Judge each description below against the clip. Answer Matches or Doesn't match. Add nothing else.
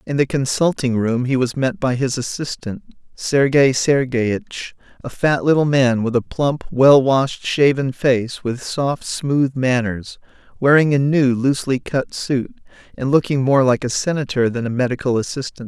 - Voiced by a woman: Doesn't match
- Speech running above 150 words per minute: Matches